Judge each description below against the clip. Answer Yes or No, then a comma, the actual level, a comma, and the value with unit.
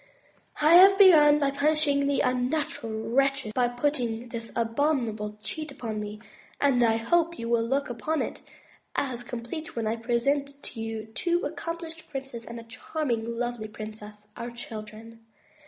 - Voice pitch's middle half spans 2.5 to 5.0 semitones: Yes, average, 4.4 semitones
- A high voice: Yes, high, 245 Hz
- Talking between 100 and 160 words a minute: Yes, average, 155 wpm